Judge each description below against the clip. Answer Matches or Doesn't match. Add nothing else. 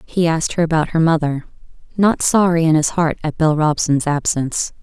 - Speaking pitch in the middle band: Matches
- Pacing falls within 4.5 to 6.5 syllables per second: Matches